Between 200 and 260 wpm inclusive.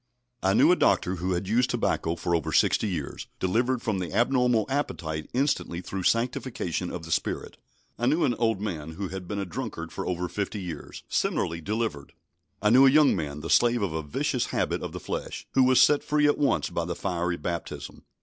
Yes: fast, 205 wpm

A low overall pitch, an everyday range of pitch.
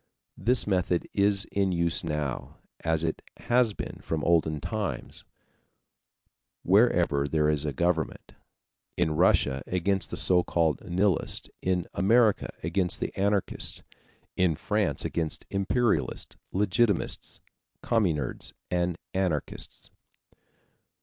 Yes: very low, 90 Hz; average, 3.7 semitones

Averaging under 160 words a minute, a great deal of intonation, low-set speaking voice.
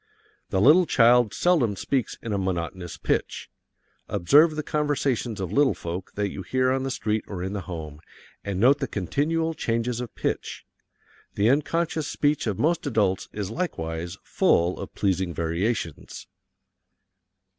Yes: average, 150 wpm; wide, 7.1 semitones; low, 110 Hz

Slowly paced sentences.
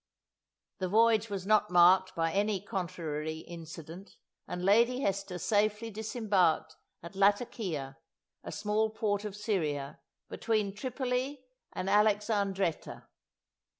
Yes: slow, 110 wpm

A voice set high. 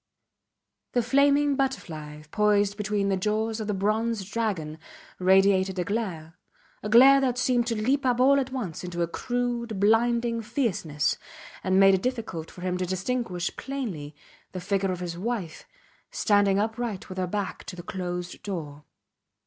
Yes: high, 205 Hz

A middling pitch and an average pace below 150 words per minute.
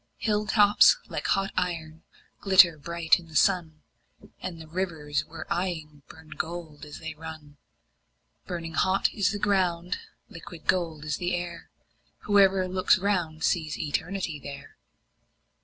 Yes: medium, 170 Hz; average, 140 wpm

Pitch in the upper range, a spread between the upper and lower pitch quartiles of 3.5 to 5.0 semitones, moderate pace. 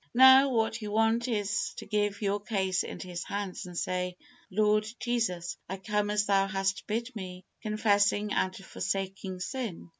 No: high, 205 Hz; narrow, 2.4 semitones; average, 160 wpm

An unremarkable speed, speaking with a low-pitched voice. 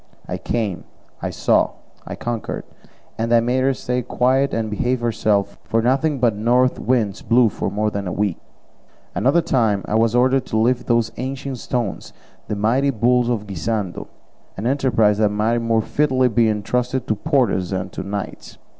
Yes: average, 170 wpm; low, 115 Hz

